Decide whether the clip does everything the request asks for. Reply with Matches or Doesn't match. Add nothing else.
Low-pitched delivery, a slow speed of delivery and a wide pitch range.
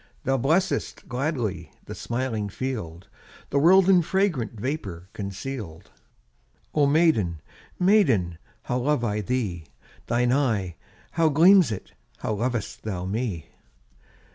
Matches